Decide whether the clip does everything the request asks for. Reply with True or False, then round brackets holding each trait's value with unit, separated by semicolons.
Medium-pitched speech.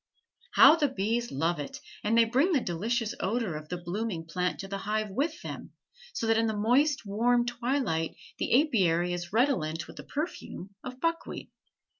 False (220 Hz)